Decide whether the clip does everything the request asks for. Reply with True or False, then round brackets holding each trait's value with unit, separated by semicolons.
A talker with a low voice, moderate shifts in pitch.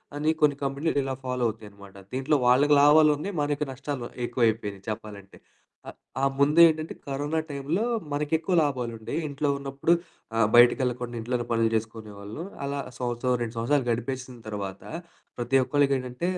True (130 Hz; 4.1 semitones)